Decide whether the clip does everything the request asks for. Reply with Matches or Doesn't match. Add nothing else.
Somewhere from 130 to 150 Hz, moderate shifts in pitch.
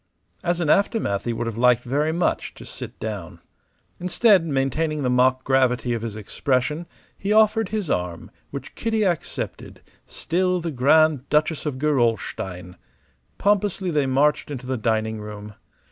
Doesn't match